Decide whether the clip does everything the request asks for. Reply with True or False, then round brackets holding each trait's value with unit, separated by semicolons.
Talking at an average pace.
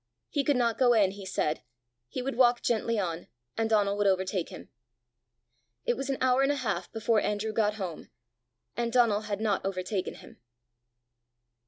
True (175 wpm)